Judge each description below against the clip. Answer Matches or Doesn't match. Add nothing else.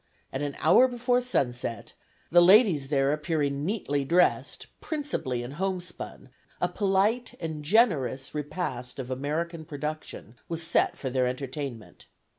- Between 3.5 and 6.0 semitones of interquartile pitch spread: Matches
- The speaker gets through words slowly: Matches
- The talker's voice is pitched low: Doesn't match